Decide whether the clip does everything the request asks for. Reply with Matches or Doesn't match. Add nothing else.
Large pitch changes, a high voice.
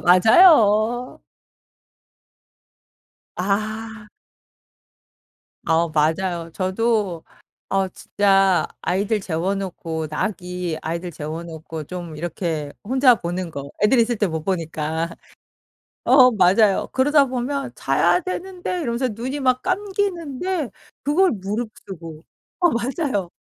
Matches